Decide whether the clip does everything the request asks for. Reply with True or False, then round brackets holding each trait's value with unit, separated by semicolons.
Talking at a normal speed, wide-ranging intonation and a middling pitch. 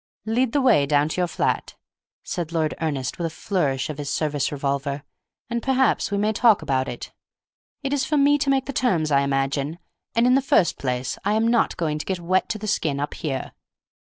False (215 wpm; 8.5 semitones; 165 Hz)